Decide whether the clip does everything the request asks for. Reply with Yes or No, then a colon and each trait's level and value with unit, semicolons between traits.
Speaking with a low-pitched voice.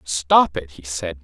Yes: very low, 90 Hz